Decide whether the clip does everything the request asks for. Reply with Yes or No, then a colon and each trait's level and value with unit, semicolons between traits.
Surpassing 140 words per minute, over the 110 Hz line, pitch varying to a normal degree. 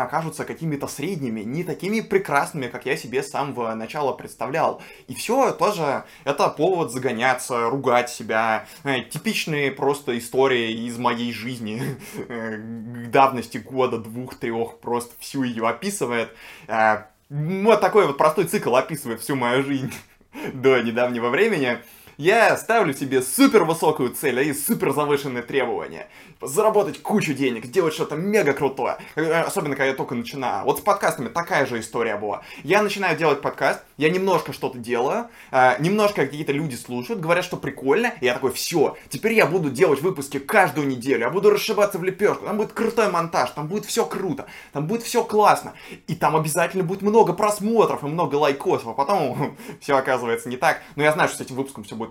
No: fast, 160 wpm; medium, 140 Hz; wide, 7.2 semitones